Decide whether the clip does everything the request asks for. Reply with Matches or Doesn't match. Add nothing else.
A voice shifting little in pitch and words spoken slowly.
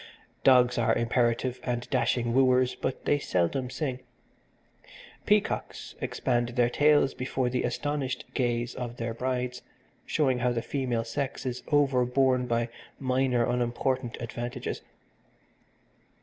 Matches